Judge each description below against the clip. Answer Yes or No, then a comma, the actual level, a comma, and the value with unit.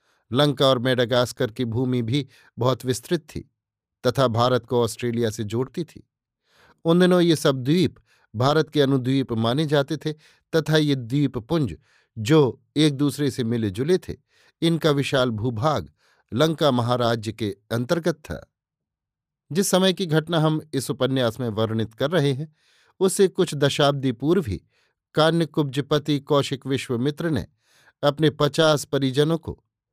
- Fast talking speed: No, average, 140 wpm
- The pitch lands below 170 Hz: Yes, medium, 140 Hz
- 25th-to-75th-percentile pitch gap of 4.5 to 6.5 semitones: No, average, 4.1 semitones